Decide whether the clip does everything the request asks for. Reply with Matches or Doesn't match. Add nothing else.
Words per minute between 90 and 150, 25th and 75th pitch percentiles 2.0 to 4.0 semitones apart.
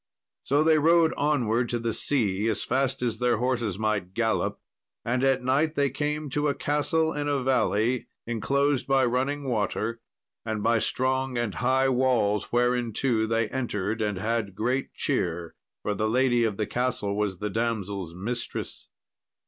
Doesn't match